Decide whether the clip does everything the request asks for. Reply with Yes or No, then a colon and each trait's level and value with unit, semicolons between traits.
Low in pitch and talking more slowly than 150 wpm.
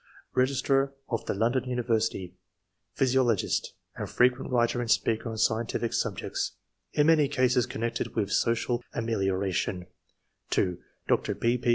Yes: low, 120 Hz; average, 140 wpm